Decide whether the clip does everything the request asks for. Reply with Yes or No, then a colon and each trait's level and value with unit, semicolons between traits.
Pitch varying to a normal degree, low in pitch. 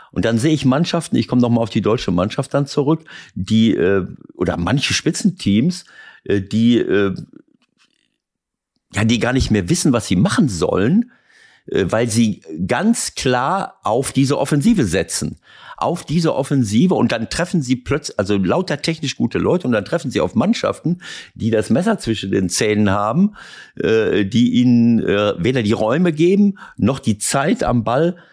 No: wide, 7.4 semitones; low, 125 Hz